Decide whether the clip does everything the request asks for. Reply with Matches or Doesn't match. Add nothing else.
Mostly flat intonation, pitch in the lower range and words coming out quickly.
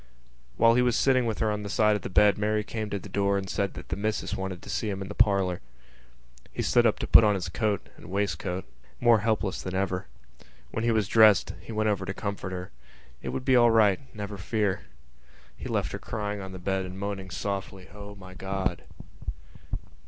Matches